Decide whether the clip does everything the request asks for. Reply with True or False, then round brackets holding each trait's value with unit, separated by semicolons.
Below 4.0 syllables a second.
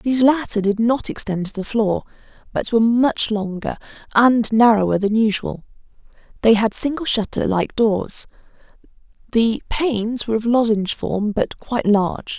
False (4.9 syllables/s)